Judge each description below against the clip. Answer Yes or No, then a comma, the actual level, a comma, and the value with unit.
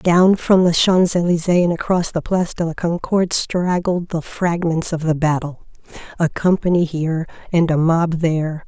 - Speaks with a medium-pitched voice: Yes, medium, 170 Hz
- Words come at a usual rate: Yes, average, 175 wpm